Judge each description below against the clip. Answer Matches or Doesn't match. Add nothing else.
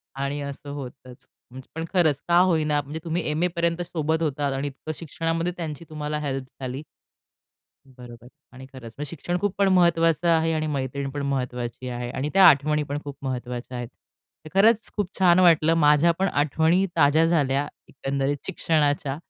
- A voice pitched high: Doesn't match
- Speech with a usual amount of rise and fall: Matches